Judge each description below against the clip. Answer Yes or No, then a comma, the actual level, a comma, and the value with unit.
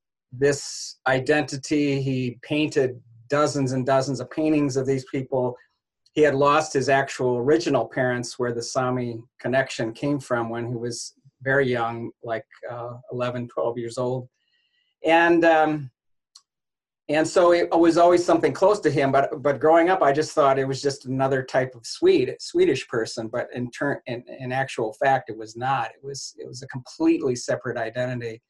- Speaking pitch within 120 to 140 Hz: Yes, low, 135 Hz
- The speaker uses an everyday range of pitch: Yes, average, 3.6 semitones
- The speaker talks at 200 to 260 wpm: No, average, 170 wpm